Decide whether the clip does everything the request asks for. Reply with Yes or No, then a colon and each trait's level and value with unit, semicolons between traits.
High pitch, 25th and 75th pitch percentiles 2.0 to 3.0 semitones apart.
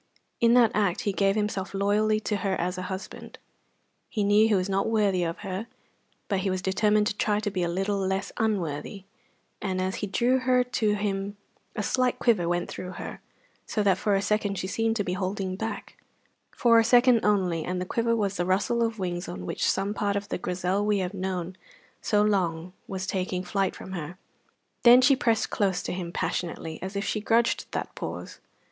Yes: high, 200 Hz; narrow, 2.5 semitones